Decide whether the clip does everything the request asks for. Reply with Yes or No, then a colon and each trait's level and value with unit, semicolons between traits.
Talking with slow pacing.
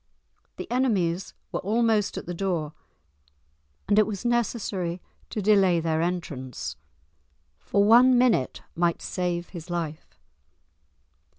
Yes: slow, 115 wpm